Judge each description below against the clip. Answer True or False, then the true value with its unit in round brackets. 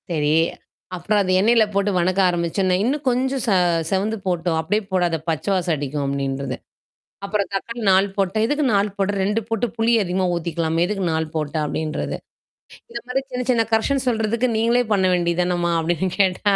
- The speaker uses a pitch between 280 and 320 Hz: False (190 Hz)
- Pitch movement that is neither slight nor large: True (4.6 semitones)